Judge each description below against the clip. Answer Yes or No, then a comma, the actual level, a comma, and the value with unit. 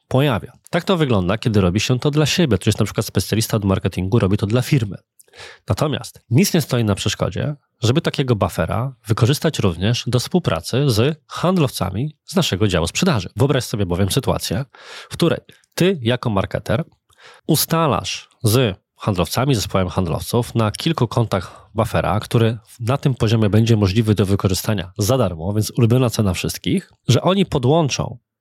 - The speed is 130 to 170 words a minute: Yes, fast, 160 wpm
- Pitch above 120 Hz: No, low, 115 Hz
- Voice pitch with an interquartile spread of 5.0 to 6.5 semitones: Yes, average, 5.3 semitones